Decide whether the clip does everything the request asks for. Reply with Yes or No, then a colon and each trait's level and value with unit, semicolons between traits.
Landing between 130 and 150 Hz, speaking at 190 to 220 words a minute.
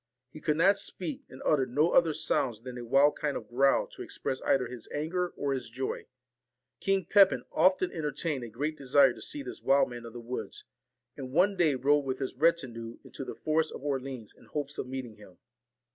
Yes: medium, 140 Hz; fast, 205 wpm